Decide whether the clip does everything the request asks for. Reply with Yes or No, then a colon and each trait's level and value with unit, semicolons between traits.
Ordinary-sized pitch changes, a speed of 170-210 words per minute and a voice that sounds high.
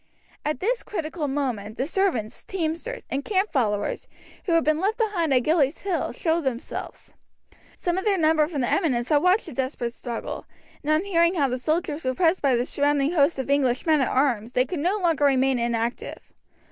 Yes: average, 4.9 semitones; average, 195 wpm; very high, 295 Hz